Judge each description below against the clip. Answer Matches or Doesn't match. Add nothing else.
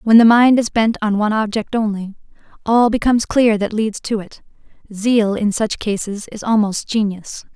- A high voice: Matches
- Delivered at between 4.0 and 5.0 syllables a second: Matches